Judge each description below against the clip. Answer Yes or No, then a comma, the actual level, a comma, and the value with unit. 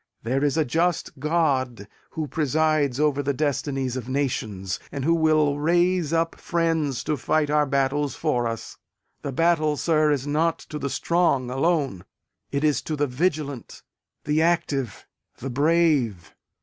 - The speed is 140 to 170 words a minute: Yes, average, 150 wpm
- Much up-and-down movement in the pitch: No, average, 3.0 semitones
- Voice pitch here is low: No, medium, 145 Hz